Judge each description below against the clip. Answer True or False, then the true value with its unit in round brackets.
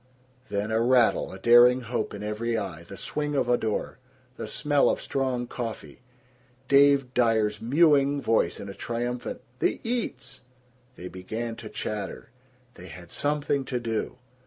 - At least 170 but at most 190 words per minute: False (155 wpm)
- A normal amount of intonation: True (4.2 semitones)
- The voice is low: True (120 Hz)